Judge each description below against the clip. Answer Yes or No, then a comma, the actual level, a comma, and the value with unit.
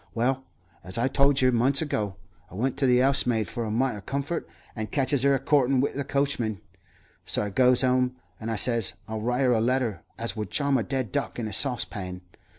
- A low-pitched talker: Yes, low, 125 Hz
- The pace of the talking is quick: Yes, fast, 220 wpm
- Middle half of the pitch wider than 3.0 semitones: Yes, average, 3.4 semitones